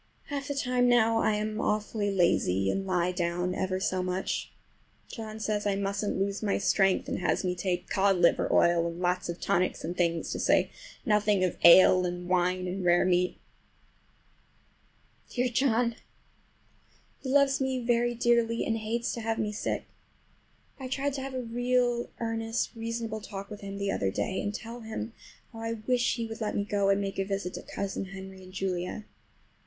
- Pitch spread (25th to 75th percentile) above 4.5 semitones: No, average, 3.9 semitones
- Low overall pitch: No, high, 205 Hz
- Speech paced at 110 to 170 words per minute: No, average, 185 wpm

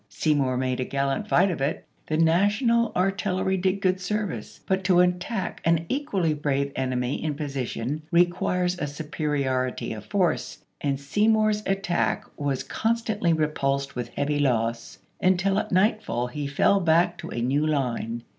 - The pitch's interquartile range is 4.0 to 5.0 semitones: No, wide, 5.6 semitones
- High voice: No, medium, 160 Hz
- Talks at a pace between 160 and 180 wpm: Yes, average, 170 wpm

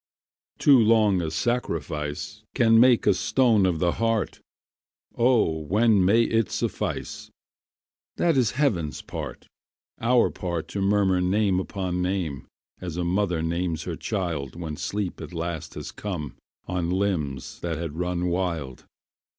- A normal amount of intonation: Yes, average, 4.3 semitones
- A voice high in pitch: No, very low, 90 Hz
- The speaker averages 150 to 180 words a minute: No, average, 140 wpm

